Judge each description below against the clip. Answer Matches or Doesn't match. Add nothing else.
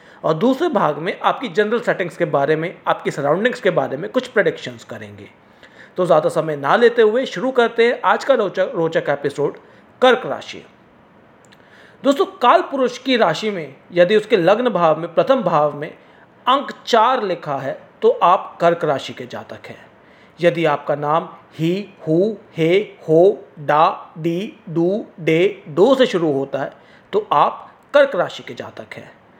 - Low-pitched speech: Doesn't match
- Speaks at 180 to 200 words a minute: Doesn't match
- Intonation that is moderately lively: Doesn't match